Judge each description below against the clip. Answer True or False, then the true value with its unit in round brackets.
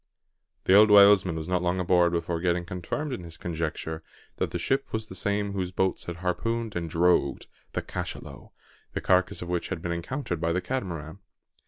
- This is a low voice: True (90 Hz)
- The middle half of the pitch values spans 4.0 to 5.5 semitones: False (2.8 semitones)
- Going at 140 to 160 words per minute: False (190 wpm)